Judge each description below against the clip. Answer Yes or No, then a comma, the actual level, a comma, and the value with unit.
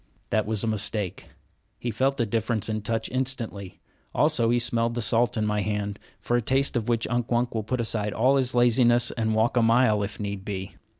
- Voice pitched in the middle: No, low, 115 Hz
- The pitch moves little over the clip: Yes, narrow, 2.3 semitones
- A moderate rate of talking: No, fast, 220 wpm